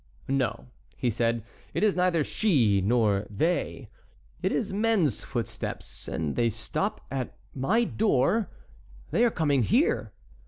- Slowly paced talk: Yes, slow, 125 wpm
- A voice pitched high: No, low, 135 Hz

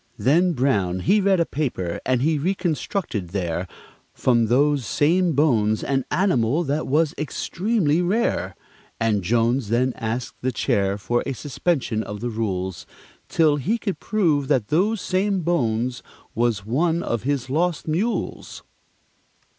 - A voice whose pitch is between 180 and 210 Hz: No, low, 135 Hz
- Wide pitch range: Yes, wide, 7.1 semitones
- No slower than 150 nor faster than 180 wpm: No, average, 140 wpm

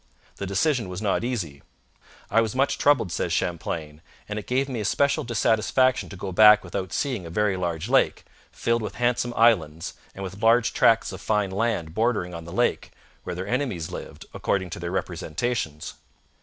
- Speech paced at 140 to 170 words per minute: No, average, 180 wpm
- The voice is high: No, low, 105 Hz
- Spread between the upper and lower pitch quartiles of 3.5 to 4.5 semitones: No, average, 5.1 semitones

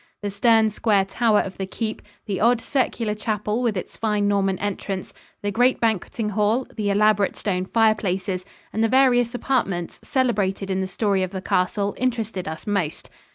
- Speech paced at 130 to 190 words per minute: Yes, average, 170 wpm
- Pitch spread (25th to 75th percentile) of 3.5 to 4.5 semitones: No, average, 2.7 semitones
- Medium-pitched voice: No, high, 210 Hz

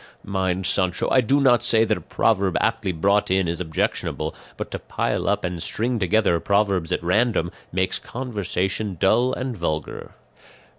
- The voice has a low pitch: Yes, low, 100 Hz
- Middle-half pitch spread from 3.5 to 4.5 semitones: Yes, average, 3.8 semitones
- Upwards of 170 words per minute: No, average, 160 wpm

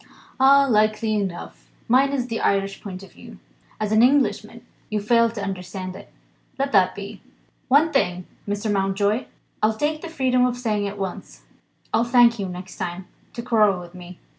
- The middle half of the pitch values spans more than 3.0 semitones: Yes, average, 4.2 semitones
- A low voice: No, high, 215 Hz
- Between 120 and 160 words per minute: No, average, 170 wpm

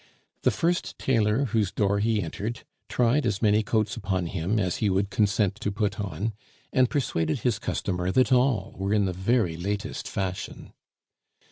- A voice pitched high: No, low, 105 Hz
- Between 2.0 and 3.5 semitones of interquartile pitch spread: Yes, average, 3.2 semitones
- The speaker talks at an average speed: Yes, average, 165 wpm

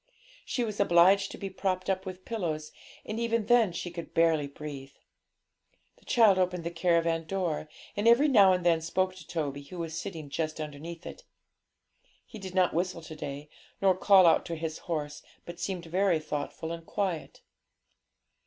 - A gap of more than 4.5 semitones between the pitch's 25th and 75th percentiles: No, average, 3.2 semitones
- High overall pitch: No, medium, 175 Hz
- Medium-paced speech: Yes, average, 175 wpm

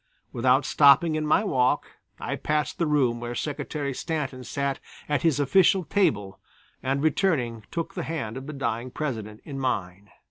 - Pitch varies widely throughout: No, average, 4.1 semitones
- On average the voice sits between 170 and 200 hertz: No, medium, 140 Hz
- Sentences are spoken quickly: No, average, 165 wpm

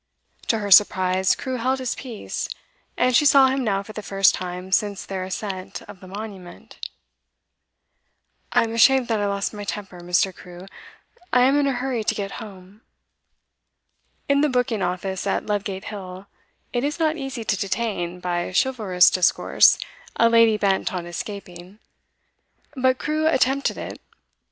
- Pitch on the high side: Yes, high, 205 Hz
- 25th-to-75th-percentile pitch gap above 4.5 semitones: Yes, average, 5.0 semitones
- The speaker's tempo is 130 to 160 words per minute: Yes, average, 155 wpm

